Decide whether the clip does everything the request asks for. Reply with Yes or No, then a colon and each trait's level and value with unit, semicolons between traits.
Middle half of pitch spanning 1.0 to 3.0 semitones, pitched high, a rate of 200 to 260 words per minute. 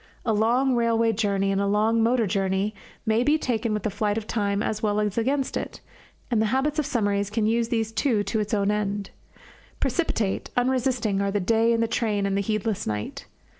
Yes: narrow, 2.4 semitones; high, 220 Hz; fast, 205 wpm